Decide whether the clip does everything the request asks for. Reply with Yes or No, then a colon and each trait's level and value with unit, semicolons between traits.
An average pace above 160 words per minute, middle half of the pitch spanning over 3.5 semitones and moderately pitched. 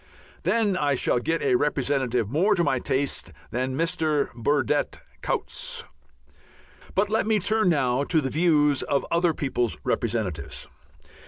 No: average, 140 wpm; average, 5.2 semitones; medium, 145 Hz